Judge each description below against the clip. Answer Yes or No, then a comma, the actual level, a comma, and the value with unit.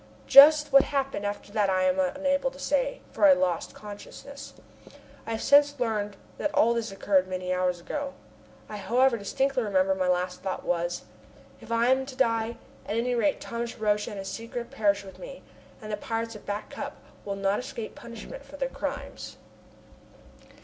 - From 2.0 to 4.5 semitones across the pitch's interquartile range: No, average, 5.3 semitones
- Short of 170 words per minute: No, average, 185 wpm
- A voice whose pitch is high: Yes, high, 225 Hz